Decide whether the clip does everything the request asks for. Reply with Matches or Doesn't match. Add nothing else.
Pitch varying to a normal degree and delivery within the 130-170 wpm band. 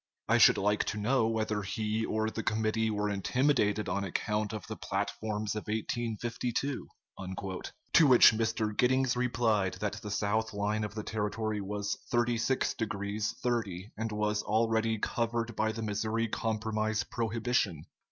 Doesn't match